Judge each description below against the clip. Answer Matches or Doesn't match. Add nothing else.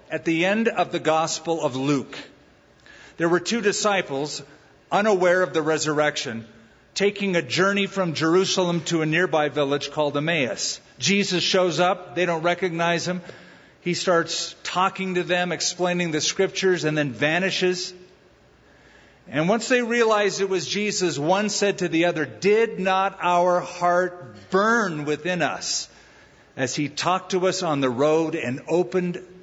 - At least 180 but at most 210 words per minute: Doesn't match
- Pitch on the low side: Doesn't match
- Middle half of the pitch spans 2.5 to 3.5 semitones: Matches